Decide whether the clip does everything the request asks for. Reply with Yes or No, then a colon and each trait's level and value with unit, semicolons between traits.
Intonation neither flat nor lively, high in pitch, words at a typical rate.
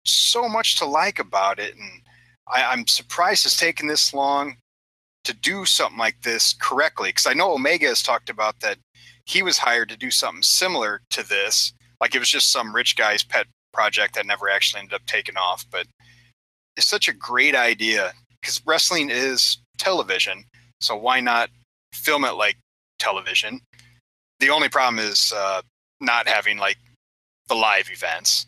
No: average, 3.9 semitones; low, 120 Hz; average, 170 wpm